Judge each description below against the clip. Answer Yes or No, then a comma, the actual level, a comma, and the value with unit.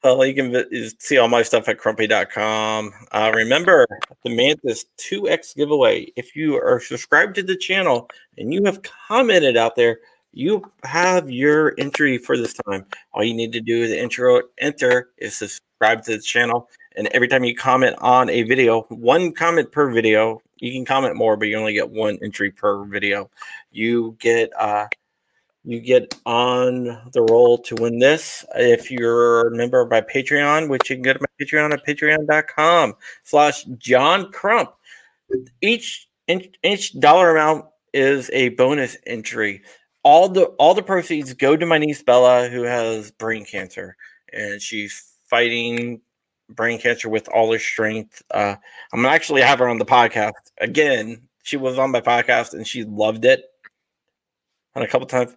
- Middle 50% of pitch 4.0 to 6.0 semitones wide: Yes, average, 4.9 semitones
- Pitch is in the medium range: No, low, 125 Hz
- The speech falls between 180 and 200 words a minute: No, average, 170 wpm